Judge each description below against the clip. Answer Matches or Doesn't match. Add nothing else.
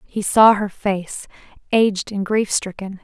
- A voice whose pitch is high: Matches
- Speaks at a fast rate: Doesn't match